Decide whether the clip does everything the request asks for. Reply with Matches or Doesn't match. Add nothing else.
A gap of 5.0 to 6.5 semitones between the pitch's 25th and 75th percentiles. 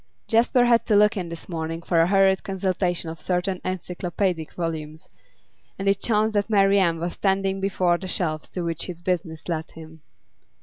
Doesn't match